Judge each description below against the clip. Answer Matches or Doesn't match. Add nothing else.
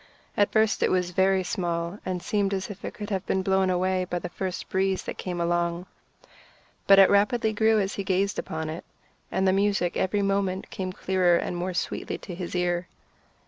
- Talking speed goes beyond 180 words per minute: Matches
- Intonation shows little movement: Matches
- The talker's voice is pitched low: Doesn't match